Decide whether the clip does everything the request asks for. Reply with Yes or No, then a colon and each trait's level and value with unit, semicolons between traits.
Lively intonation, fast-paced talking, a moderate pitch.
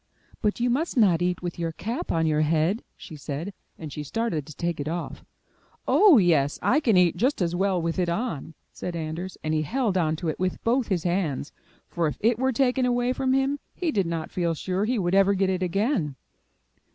Yes: wide, 6.0 semitones; fast, 220 wpm; medium, 180 Hz